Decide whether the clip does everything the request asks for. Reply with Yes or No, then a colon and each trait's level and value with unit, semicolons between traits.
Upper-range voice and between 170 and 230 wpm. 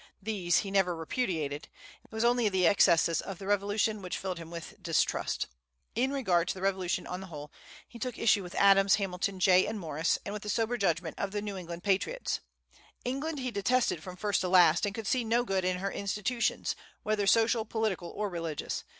Yes: high, 195 Hz; average, 200 wpm